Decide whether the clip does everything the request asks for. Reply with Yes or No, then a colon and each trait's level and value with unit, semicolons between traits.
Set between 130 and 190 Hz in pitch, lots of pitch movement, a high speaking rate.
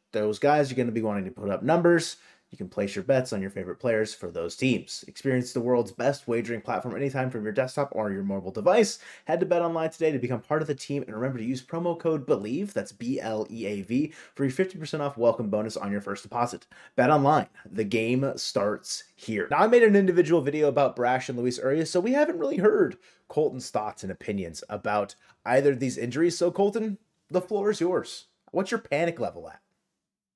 Yes: medium, 140 Hz; wide, 6.5 semitones; fast, 225 wpm